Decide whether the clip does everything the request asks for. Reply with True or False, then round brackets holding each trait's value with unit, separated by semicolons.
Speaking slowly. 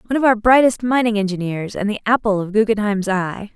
False (205 wpm)